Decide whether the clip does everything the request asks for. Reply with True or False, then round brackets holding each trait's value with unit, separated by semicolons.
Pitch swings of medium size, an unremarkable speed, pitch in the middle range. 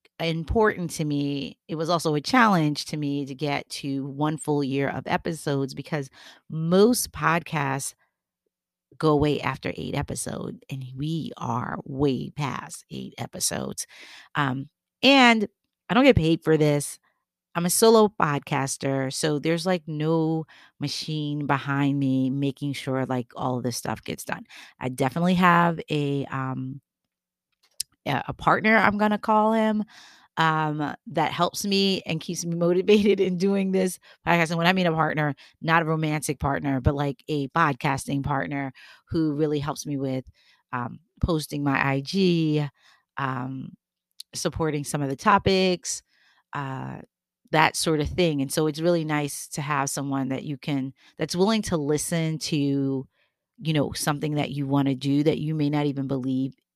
True (3.4 semitones; 160 wpm; 150 Hz)